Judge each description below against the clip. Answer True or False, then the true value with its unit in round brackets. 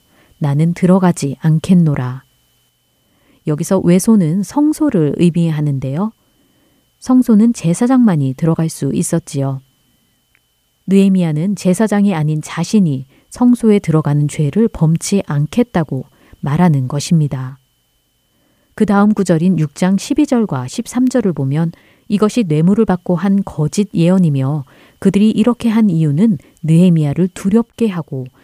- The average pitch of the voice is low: False (175 Hz)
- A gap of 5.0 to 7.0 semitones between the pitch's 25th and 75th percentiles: True (5.6 semitones)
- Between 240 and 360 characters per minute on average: True (265 characters per minute)